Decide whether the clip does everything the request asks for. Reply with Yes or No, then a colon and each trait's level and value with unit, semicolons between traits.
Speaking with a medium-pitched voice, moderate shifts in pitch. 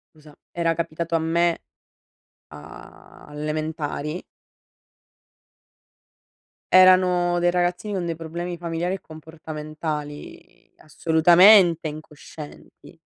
No: medium, 165 Hz; narrow, 2.3 semitones